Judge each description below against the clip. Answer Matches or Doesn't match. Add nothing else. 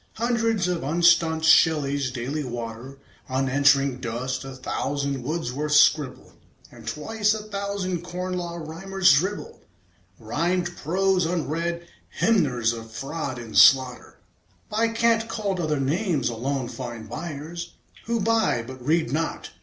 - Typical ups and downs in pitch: Doesn't match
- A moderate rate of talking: Doesn't match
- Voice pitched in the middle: Matches